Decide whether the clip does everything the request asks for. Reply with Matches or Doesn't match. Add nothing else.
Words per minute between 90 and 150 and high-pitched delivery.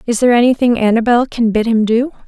Doesn't match